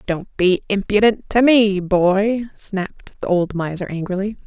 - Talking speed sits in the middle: Yes, average, 150 wpm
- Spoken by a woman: Yes, female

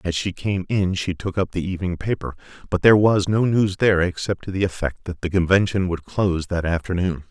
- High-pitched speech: No, very low, 90 Hz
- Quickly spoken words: Yes, fast, 220 wpm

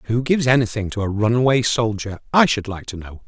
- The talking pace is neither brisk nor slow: No, fast, 220 wpm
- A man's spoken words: Yes, male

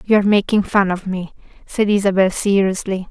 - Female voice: Yes, female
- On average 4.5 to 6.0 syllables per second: Yes, 5.2 syllables/s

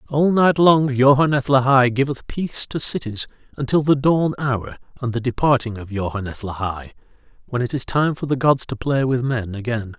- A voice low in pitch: Yes, low, 130 Hz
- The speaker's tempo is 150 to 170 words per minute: No, average, 185 wpm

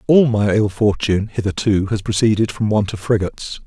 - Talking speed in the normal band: Yes, average, 180 wpm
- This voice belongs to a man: Yes, male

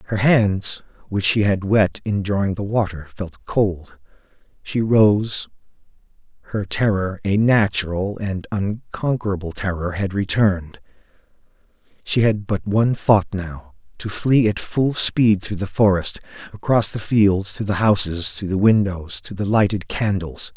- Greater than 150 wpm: No, average, 145 wpm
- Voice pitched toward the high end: No, low, 100 Hz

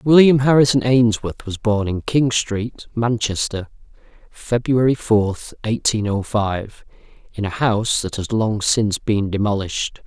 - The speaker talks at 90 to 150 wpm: Yes, slow, 135 wpm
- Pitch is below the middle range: Yes, low, 110 Hz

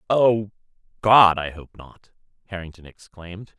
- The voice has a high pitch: No, very low, 95 Hz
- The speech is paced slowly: Yes, slow, 115 wpm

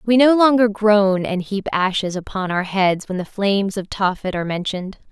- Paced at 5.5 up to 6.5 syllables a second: No, 5.1 syllables/s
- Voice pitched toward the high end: Yes, high, 200 Hz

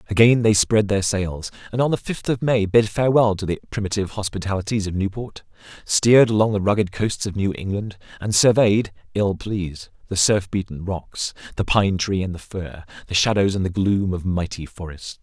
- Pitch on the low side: Yes, low, 100 Hz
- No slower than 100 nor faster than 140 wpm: No, average, 195 wpm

